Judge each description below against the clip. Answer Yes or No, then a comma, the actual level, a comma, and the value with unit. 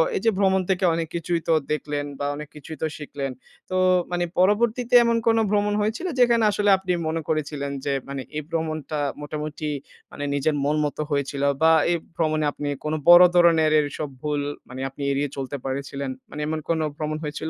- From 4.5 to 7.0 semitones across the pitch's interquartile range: No, average, 3.7 semitones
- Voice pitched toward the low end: No, medium, 155 Hz